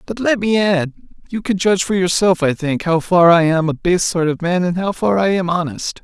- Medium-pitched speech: Yes, medium, 180 Hz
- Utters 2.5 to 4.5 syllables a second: No, 5.3 syllables/s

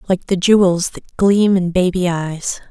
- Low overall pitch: No, medium, 185 Hz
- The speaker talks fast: No, average, 175 wpm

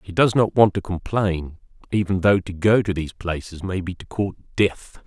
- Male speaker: Yes, male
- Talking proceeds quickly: Yes, fast, 215 wpm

